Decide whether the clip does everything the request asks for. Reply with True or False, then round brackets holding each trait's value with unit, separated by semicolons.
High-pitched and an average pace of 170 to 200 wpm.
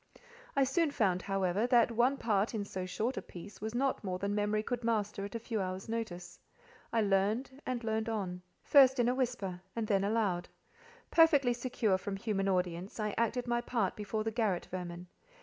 True (215 Hz; 190 wpm)